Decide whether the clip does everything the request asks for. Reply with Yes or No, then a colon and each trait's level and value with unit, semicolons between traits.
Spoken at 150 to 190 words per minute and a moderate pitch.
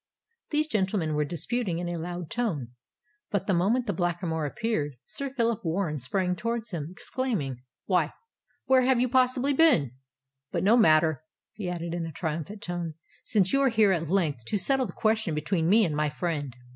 Yes: average, 185 wpm; medium, 180 Hz